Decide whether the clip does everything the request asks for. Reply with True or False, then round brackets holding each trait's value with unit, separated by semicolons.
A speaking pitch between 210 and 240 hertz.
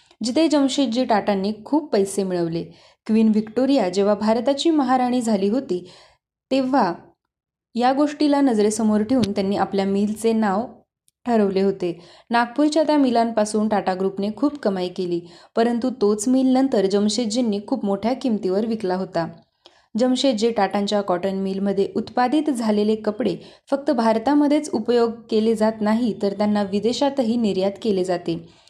True (220 Hz)